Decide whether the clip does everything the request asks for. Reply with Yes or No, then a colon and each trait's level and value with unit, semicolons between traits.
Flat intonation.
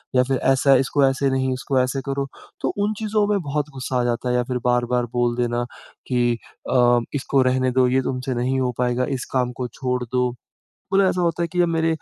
Yes: narrow, 2.0 semitones